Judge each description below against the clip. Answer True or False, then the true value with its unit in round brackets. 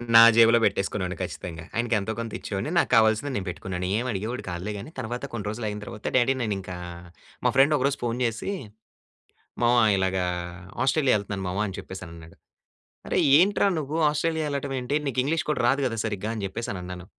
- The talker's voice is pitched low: True (115 Hz)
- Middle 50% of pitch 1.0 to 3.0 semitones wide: False (5.5 semitones)